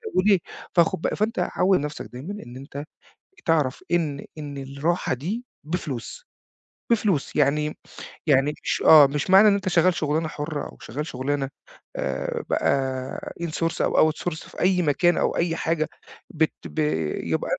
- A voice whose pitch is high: No, medium, 155 Hz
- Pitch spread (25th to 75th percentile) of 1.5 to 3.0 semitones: No, average, 4.0 semitones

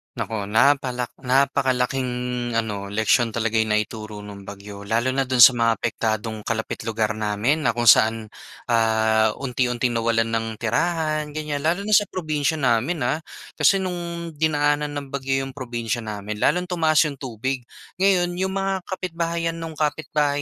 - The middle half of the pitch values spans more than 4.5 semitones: Yes, wide, 5.6 semitones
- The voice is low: Yes, low, 130 Hz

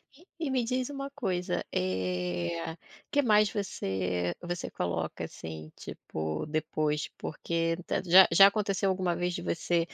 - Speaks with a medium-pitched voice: Yes, medium, 170 Hz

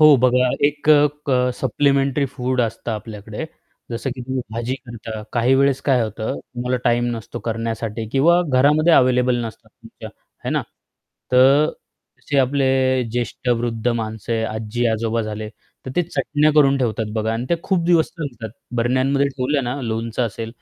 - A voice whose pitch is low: Yes, low, 125 Hz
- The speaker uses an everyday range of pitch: Yes, average, 3.3 semitones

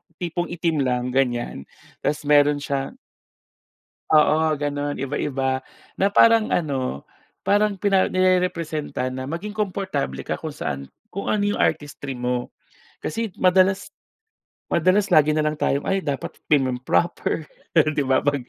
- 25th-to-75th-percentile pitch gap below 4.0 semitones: No, wide, 5.4 semitones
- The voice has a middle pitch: Yes, medium, 150 Hz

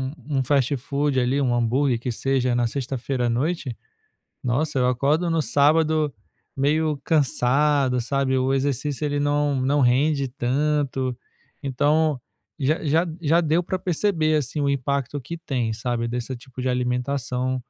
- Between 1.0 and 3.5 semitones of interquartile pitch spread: Yes, average, 3.0 semitones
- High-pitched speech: No, medium, 140 Hz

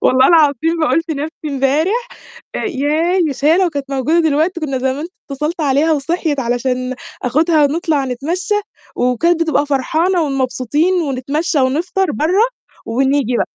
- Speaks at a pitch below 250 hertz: No, very high, 295 Hz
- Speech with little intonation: No, average, 3.8 semitones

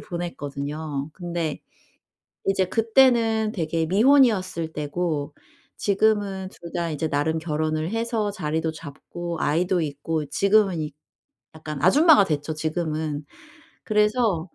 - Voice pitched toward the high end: No, medium, 170 Hz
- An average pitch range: Yes, average, 4.7 semitones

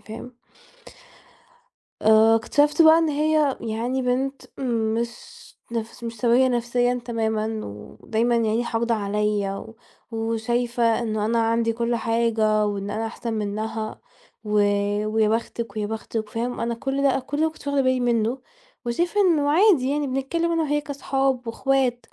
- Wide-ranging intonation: No, average, 3.3 semitones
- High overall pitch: Yes, high, 235 Hz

